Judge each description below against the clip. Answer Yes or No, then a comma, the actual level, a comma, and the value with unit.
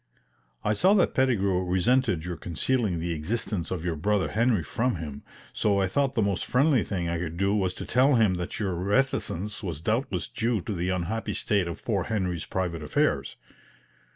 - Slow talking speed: No, average, 185 wpm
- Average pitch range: Yes, average, 4.6 semitones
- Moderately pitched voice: No, very low, 95 Hz